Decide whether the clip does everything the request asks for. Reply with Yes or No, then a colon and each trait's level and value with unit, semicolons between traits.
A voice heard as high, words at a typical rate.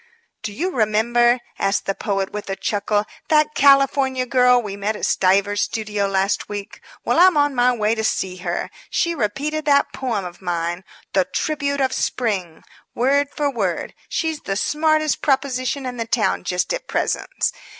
Yes: high, 235 Hz; average, 170 wpm